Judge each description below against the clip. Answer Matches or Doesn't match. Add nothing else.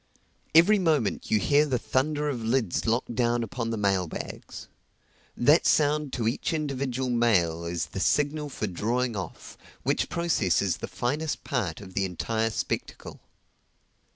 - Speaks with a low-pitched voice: Matches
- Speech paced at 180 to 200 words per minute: Doesn't match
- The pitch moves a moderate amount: Doesn't match